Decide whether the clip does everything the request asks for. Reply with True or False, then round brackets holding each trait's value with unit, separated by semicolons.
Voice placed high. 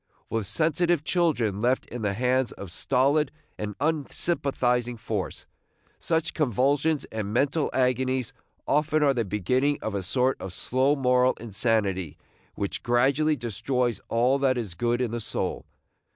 False (125 Hz)